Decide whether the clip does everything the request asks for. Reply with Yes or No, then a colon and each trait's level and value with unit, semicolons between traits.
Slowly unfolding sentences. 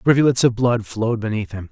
No: fast, 210 wpm